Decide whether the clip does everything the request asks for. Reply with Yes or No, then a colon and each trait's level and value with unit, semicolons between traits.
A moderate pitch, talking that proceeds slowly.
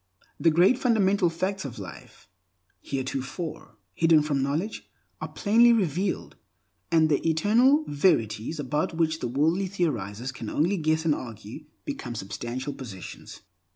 Yes: medium, 155 Hz; slow, 130 wpm